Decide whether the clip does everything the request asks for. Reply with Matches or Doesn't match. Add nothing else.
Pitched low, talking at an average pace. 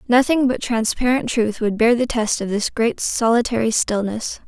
Doesn't match